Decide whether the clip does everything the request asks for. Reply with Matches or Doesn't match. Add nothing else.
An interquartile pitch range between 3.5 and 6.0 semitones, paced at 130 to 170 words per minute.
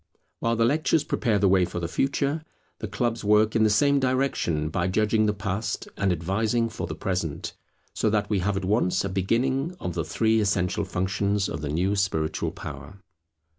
Doesn't match